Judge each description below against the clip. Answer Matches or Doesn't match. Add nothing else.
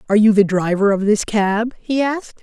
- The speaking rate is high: Matches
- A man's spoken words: Doesn't match